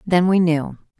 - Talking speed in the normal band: Yes, average, 180 wpm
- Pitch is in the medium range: Yes, medium, 170 Hz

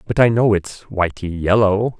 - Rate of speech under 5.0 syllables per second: Yes, 4.4 syllables/s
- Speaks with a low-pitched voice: Yes, low, 100 Hz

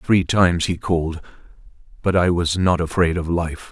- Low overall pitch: Yes, very low, 85 Hz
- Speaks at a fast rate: No, average, 160 wpm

